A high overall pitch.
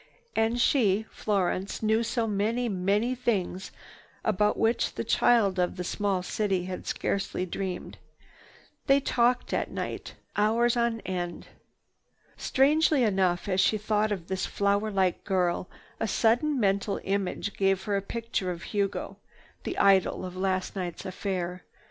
Yes: high, 200 Hz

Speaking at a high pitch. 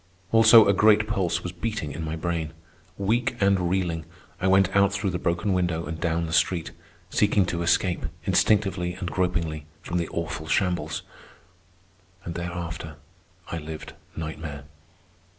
No: very low, 90 Hz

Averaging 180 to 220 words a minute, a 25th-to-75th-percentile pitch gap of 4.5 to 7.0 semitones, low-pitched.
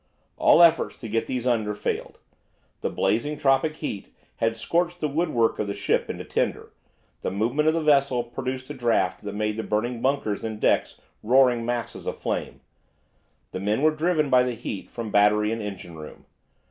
Yes: average, 185 wpm; average, 4.9 semitones; low, 120 Hz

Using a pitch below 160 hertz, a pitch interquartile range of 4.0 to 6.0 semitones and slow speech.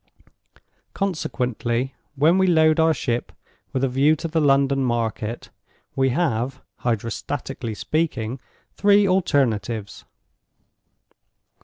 Yes: low, 135 Hz; average, 5.1 semitones; slow, 100 wpm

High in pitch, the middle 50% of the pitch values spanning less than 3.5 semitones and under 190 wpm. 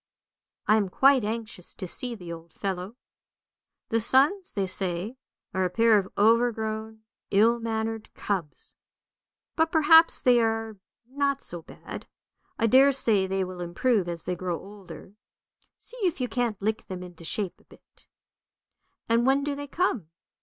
No: high, 220 Hz; average, 4.9 semitones; average, 155 wpm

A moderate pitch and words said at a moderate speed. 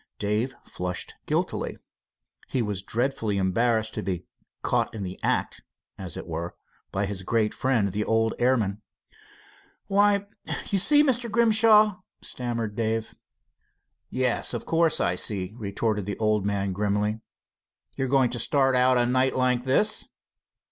No: low, 115 Hz; average, 145 wpm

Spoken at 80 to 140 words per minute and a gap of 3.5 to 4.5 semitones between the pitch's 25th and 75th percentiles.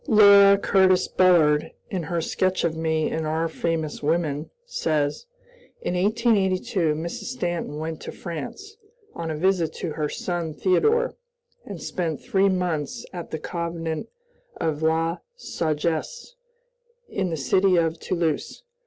No: slow, 135 wpm; average, 3.0 semitones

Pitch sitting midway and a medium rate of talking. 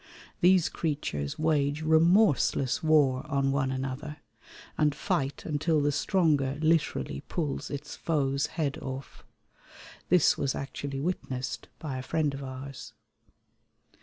No: medium, 145 Hz; slow, 120 wpm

